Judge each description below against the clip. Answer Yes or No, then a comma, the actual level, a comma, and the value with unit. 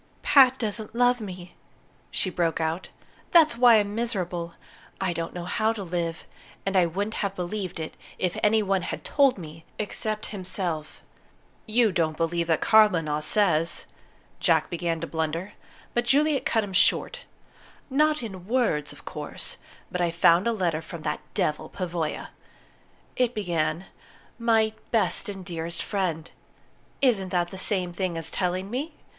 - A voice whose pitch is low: No, medium, 185 Hz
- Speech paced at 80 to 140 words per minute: No, average, 155 wpm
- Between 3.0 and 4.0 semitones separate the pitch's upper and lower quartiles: No, average, 4.5 semitones